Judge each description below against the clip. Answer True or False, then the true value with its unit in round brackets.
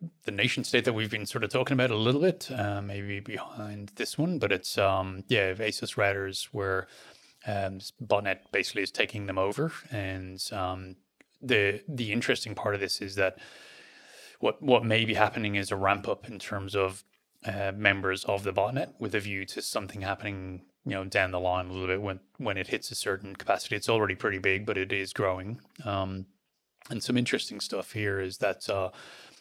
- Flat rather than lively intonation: True (2.3 semitones)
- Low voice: True (100 Hz)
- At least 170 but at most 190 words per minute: False (200 wpm)